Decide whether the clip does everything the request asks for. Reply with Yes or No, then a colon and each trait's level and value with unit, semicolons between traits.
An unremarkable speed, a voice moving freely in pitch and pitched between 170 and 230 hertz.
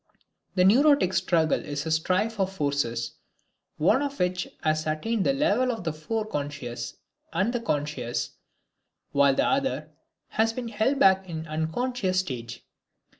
Yes: average, 150 wpm; wide, 6.8 semitones; medium, 185 Hz